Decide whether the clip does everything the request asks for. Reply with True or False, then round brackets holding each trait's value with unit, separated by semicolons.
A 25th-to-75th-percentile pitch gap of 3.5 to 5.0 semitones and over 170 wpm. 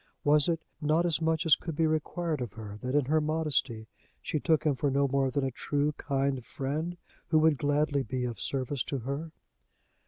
False (2.8 semitones; 200 wpm)